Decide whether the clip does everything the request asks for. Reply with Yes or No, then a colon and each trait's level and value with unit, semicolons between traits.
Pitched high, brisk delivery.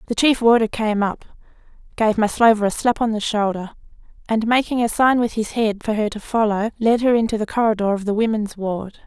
Yes: high, 220 Hz; fast, 210 wpm